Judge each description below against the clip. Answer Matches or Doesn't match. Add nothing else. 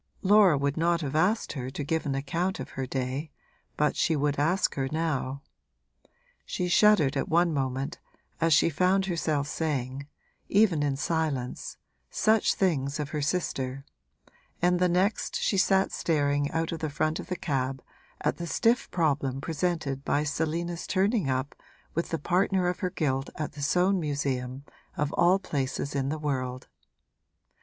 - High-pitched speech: Doesn't match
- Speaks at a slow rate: Doesn't match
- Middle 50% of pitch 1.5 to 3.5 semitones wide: Doesn't match